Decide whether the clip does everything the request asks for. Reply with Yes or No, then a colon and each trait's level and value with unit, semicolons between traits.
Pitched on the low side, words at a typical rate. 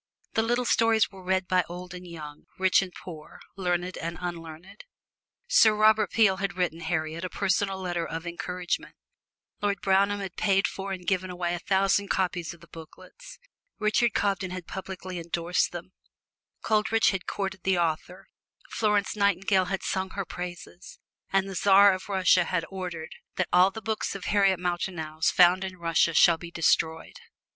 No: medium, 185 Hz; average, 170 wpm